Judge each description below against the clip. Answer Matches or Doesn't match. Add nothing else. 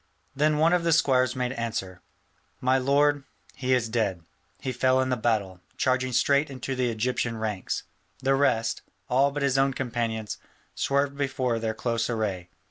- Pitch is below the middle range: Matches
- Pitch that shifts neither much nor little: Matches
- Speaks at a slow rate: Doesn't match